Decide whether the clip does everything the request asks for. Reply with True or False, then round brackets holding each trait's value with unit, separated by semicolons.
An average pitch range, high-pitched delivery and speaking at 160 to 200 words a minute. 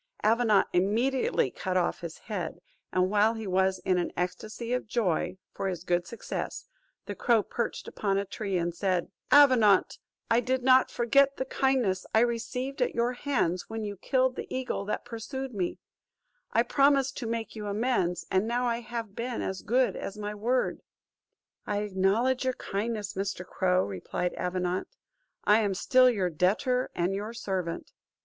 True (4.7 semitones; 215 Hz; 170 wpm)